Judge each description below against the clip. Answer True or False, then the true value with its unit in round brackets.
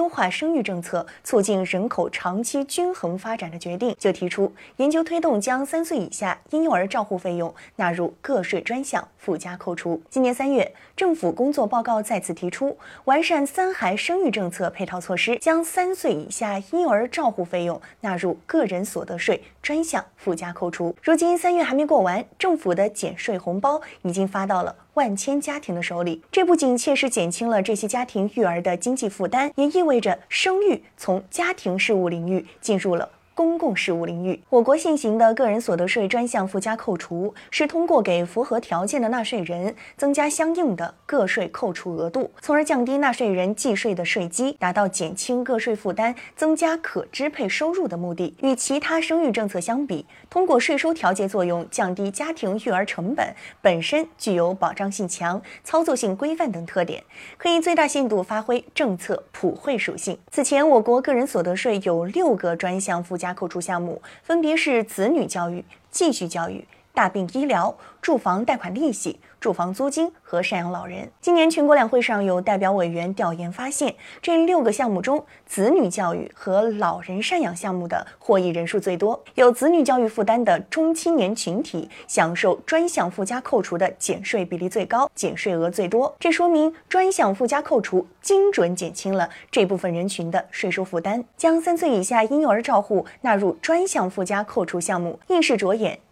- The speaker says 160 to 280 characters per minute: False (290 characters per minute)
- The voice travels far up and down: True (8.3 semitones)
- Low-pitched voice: False (225 Hz)